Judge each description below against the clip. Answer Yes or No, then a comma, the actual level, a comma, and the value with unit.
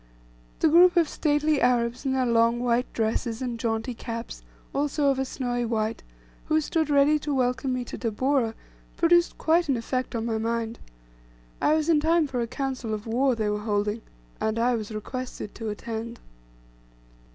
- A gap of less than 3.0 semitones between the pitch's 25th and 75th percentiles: No, average, 3.8 semitones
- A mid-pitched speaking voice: No, high, 245 Hz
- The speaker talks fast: No, average, 175 wpm